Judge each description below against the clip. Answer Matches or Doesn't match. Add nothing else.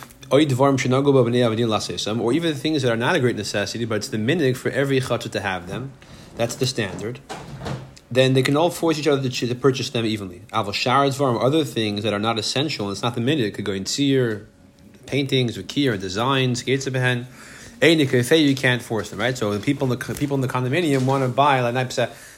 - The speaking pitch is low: Matches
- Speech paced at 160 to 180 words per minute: Doesn't match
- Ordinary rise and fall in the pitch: Matches